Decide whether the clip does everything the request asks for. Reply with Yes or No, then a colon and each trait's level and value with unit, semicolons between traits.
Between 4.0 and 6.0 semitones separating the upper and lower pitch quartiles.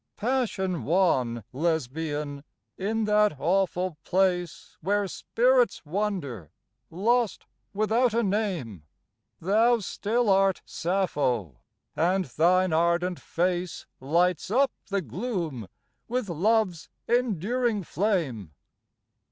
Yes: average, 4.9 semitones